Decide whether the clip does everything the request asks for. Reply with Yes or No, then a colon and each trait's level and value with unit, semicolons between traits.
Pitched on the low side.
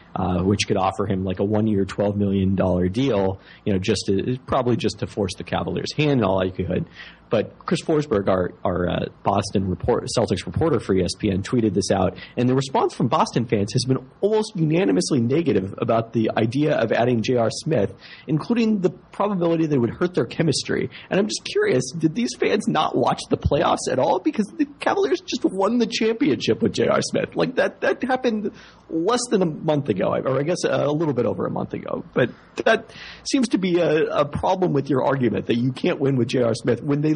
Yes: low, 130 Hz